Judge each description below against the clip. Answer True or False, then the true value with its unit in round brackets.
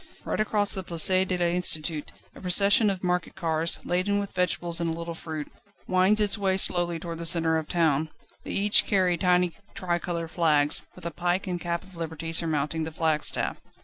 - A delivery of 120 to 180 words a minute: False (190 wpm)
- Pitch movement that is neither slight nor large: False (2.2 semitones)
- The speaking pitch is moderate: True (175 Hz)